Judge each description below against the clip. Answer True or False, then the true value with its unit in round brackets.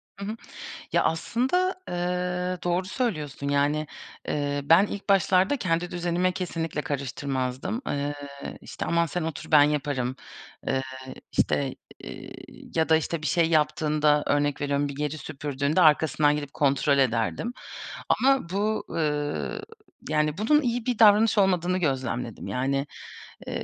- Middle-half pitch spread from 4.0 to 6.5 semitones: True (4.3 semitones)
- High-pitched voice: False (155 Hz)